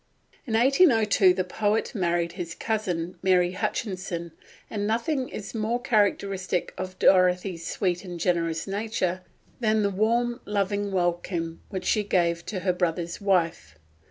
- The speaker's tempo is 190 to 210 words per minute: No, slow, 135 wpm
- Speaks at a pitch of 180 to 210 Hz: Yes, high, 190 Hz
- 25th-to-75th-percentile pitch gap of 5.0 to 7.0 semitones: No, average, 3.4 semitones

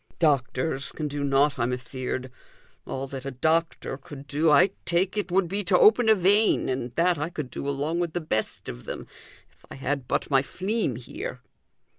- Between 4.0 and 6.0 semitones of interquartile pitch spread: Yes, average, 4.8 semitones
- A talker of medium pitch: Yes, medium, 145 Hz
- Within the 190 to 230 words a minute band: Yes, average, 195 wpm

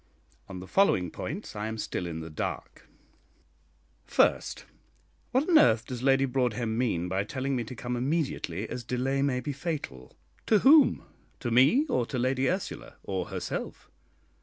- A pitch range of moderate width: Yes, average, 4.2 semitones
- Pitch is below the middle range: Yes, low, 125 Hz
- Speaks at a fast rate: No, average, 160 wpm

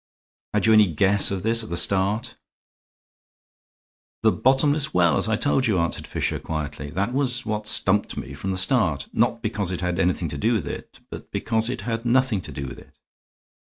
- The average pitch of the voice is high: No, low, 105 Hz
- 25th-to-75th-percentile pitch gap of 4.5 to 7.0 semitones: Yes, average, 4.9 semitones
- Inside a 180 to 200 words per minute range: Yes, average, 195 wpm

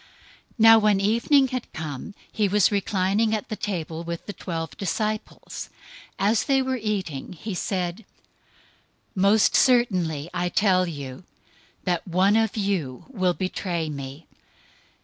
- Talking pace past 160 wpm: No, average, 140 wpm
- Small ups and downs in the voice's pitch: No, average, 4.1 semitones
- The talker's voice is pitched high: Yes, high, 195 Hz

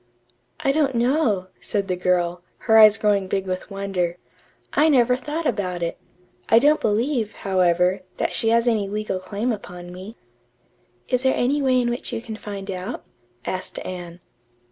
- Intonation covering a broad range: No, average, 4.8 semitones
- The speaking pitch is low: No, high, 210 Hz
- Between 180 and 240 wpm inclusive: No, average, 165 wpm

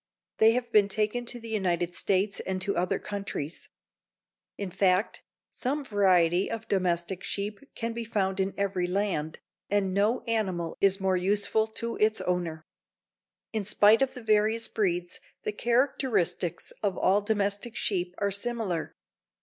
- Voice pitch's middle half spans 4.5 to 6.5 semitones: No, average, 3.1 semitones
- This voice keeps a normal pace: Yes, average, 150 wpm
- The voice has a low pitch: No, high, 200 Hz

